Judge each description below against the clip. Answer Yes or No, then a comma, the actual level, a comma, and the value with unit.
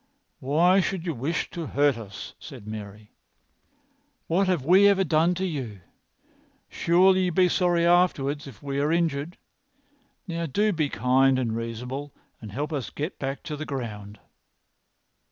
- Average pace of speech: Yes, average, 160 wpm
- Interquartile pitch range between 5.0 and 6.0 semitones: Yes, average, 5.3 semitones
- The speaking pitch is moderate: Yes, medium, 145 Hz